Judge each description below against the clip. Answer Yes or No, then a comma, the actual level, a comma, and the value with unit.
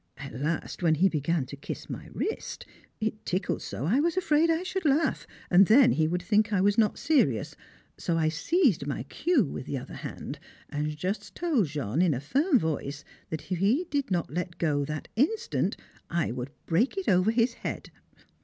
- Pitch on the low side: No, medium, 185 Hz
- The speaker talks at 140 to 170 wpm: No, average, 195 wpm